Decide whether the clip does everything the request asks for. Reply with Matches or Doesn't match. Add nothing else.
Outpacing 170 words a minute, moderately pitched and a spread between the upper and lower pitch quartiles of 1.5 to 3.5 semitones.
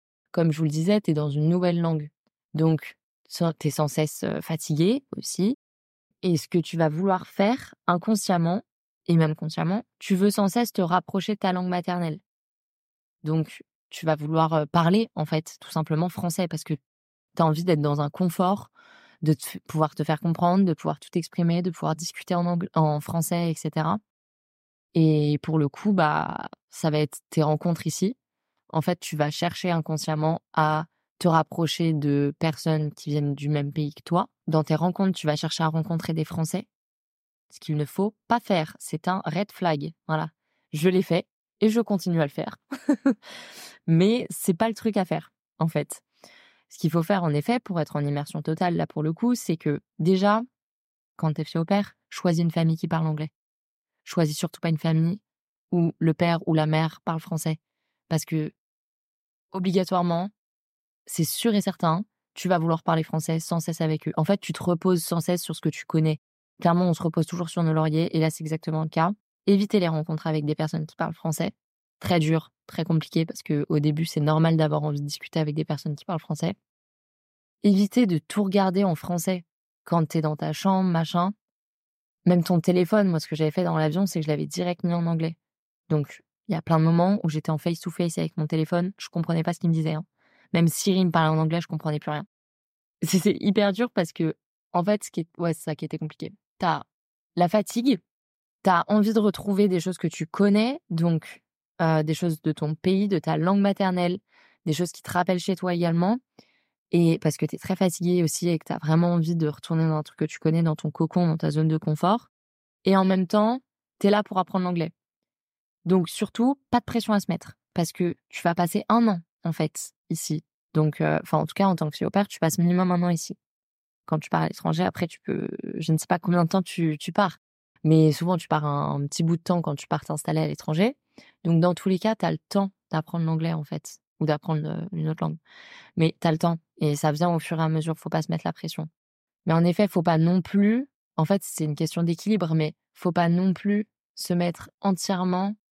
Matches